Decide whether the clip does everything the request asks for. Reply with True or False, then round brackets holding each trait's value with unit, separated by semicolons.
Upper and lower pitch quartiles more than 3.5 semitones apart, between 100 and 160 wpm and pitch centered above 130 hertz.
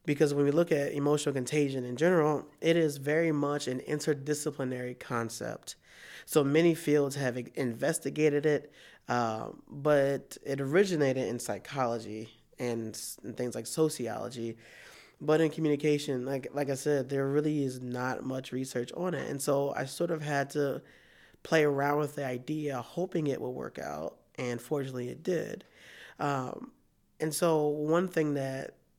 False (3.1 semitones; 155 wpm; 140 Hz)